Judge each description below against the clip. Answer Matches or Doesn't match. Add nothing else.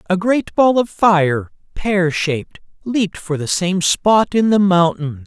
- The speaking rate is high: Doesn't match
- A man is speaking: Matches